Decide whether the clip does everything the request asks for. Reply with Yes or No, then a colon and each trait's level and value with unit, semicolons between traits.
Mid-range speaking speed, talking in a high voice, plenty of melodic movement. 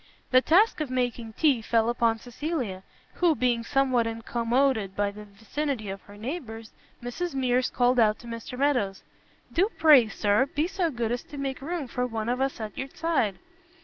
No: average, 180 wpm; high, 245 Hz; average, 3.9 semitones